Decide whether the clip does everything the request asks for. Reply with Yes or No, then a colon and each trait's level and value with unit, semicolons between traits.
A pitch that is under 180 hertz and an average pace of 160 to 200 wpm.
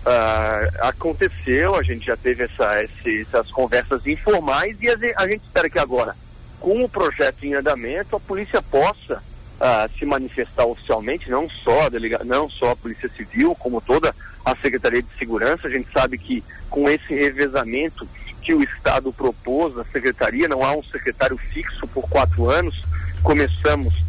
Yes: low, 135 Hz; average, 165 wpm